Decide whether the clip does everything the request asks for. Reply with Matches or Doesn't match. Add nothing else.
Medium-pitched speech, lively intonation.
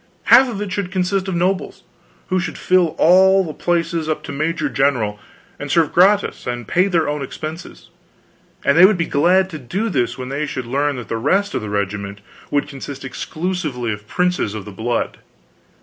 Matches